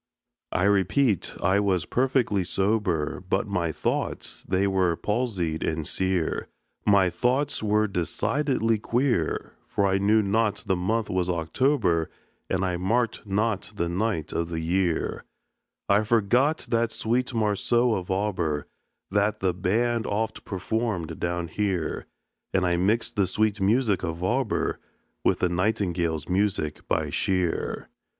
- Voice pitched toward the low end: Yes, low, 100 Hz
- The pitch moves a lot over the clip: No, average, 3.9 semitones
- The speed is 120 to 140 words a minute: Yes, slow, 135 wpm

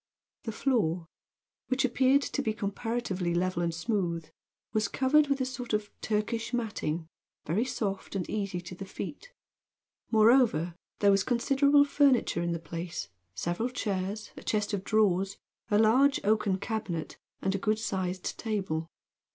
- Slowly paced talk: No, average, 150 wpm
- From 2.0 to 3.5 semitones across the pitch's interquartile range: No, average, 4.9 semitones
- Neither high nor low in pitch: No, high, 210 Hz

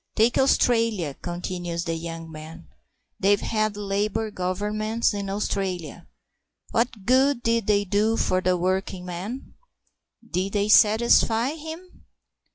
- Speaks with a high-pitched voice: Yes, high, 205 Hz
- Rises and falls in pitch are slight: No, average, 3.9 semitones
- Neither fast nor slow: No, slow, 120 wpm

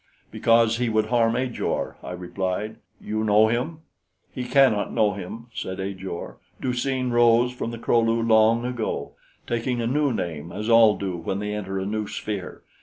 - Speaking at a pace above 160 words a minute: Yes, average, 180 wpm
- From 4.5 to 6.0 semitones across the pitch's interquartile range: No, average, 2.7 semitones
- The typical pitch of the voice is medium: No, low, 115 Hz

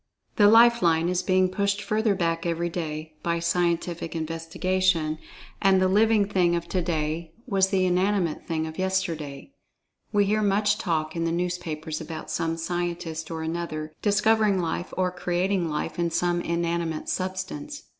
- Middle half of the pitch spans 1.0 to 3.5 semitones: Yes, average, 2.7 semitones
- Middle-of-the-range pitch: Yes, medium, 175 Hz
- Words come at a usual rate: Yes, average, 155 wpm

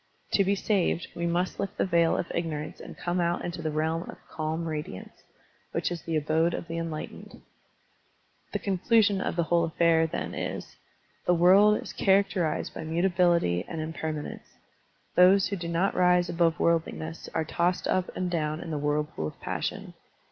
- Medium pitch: Yes, medium, 170 Hz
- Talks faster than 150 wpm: Yes, average, 175 wpm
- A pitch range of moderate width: No, narrow, 2.1 semitones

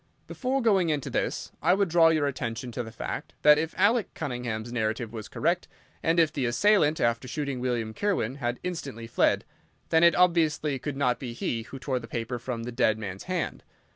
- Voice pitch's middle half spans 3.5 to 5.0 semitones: No, wide, 5.6 semitones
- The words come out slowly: No, average, 200 wpm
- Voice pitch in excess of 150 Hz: No, low, 130 Hz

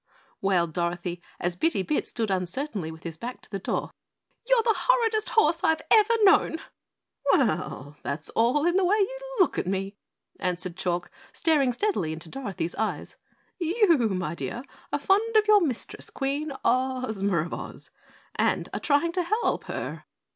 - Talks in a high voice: Yes, very high, 255 Hz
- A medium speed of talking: Yes, average, 160 wpm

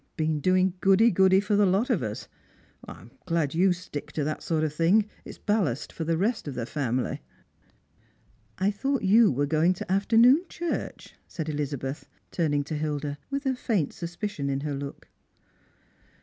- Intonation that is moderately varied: No, wide, 5.7 semitones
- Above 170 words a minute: Yes, average, 180 wpm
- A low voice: No, medium, 170 Hz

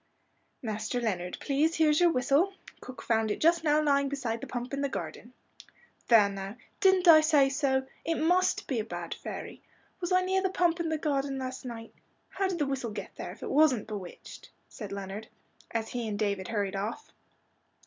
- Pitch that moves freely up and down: Yes, wide, 6.3 semitones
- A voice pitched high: Yes, very high, 265 Hz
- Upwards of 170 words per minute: Yes, average, 195 wpm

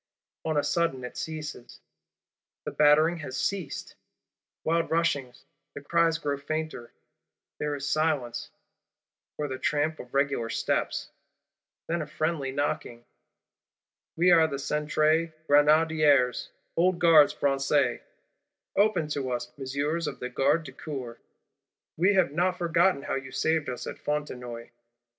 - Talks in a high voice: No, medium, 150 Hz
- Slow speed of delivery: Yes, slow, 130 wpm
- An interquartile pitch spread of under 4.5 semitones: Yes, average, 3.1 semitones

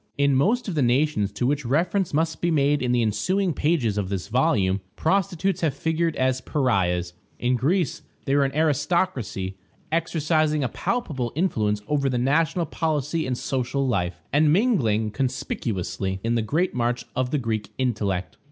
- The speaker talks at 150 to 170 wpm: Yes, average, 165 wpm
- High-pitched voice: No, low, 135 Hz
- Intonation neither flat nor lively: No, wide, 5.8 semitones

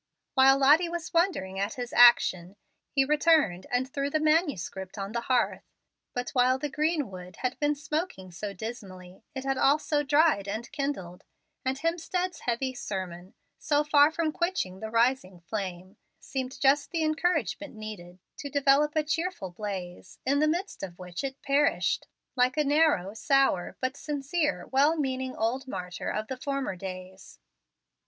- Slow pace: No, average, 155 wpm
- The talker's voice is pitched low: No, very high, 265 Hz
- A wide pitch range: Yes, wide, 7.3 semitones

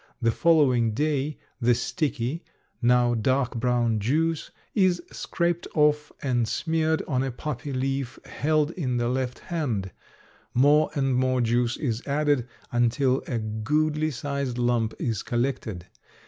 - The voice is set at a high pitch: No, low, 130 Hz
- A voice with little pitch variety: No, average, 3.9 semitones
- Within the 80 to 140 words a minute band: Yes, slow, 135 wpm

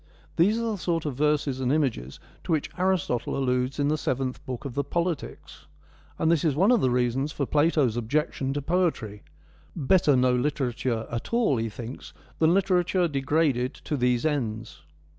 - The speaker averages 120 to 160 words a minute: No, average, 175 wpm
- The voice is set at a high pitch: No, medium, 140 Hz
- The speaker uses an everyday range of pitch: Yes, average, 4.5 semitones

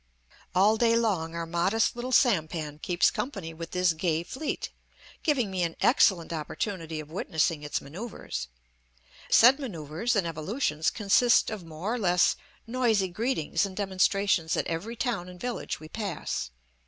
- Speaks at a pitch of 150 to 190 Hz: Yes, medium, 185 Hz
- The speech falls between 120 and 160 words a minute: Yes, average, 150 wpm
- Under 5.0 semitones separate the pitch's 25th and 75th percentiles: No, wide, 5.6 semitones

